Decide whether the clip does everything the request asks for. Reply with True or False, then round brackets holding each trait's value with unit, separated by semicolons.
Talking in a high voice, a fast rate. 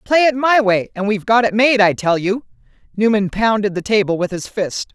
True (210 Hz; 230 wpm)